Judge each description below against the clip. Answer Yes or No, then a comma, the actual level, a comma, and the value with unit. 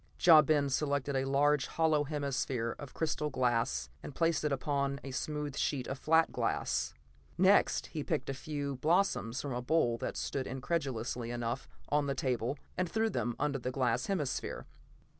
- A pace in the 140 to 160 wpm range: No, average, 170 wpm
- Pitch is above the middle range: No, medium, 140 Hz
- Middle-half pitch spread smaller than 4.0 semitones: Yes, average, 2.9 semitones